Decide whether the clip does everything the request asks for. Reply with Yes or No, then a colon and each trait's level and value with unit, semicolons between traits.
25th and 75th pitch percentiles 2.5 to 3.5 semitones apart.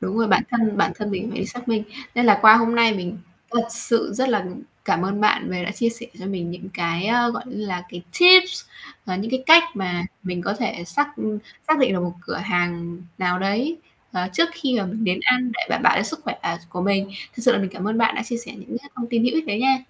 No: average, 4.7 semitones